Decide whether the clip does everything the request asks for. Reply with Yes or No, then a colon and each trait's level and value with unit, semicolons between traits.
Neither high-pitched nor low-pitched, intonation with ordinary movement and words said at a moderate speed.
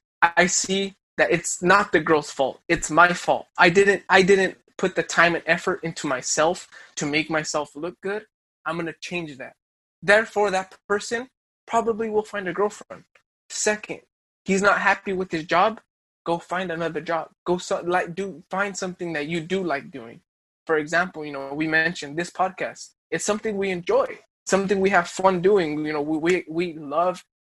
Yes: medium, 180 Hz; average, 3.2 semitones; average, 185 wpm